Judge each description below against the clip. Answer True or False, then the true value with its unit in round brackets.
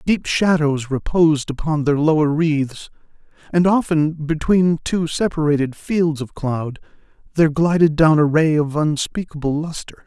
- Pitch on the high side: False (155 Hz)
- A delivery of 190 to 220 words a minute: False (135 wpm)